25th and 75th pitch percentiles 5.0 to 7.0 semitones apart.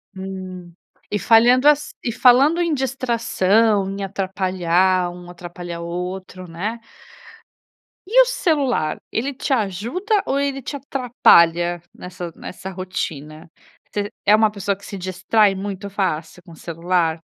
Yes: average, 5.3 semitones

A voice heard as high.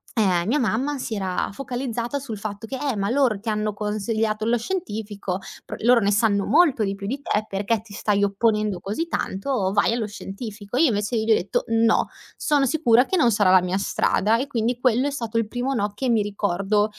Yes: high, 220 Hz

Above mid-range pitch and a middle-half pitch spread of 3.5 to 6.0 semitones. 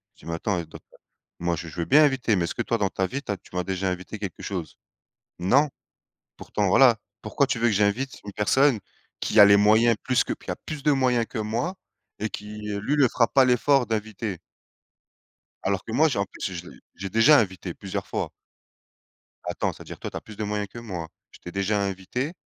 No: low, 105 Hz; average, 4.4 semitones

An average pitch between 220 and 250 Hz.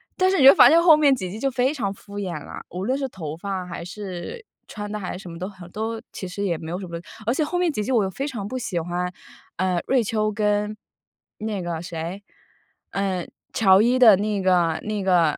No: high, 200 Hz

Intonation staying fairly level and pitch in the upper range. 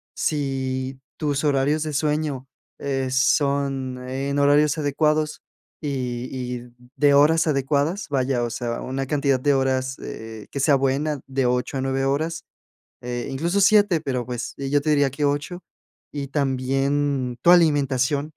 No: narrow, 2.1 semitones; medium, 140 Hz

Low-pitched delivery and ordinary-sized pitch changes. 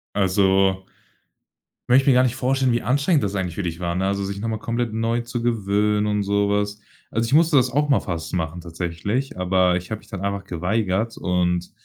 Yes: low, 100 Hz; average, 4.3 semitones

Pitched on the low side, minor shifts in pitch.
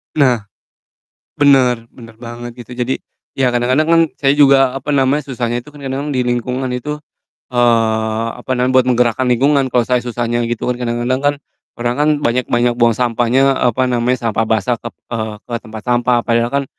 Yes: low, 125 Hz; narrow, 1.9 semitones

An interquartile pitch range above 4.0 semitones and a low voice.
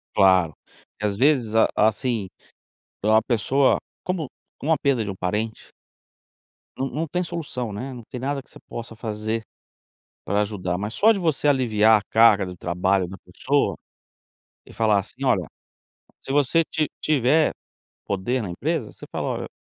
Yes: average, 5.2 semitones; low, 115 Hz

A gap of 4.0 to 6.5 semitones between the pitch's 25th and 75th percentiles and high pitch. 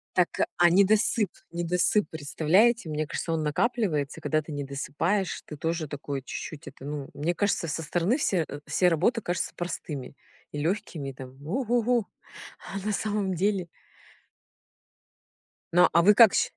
No: average, 5.3 semitones; medium, 170 Hz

